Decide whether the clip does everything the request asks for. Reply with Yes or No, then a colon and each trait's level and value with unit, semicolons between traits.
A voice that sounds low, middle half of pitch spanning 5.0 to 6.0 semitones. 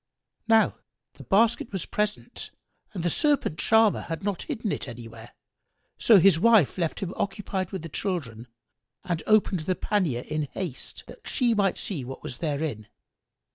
No: medium, 185 Hz; wide, 5.5 semitones